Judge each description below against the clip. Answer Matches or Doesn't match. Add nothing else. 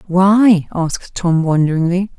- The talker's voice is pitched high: Doesn't match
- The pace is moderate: Doesn't match